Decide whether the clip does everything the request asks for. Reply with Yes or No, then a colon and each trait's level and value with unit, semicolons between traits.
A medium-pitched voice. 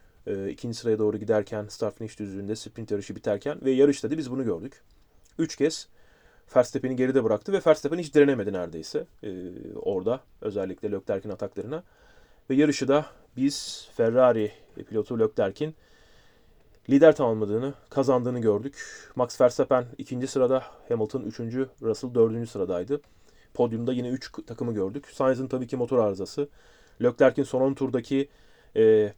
No: low, 125 Hz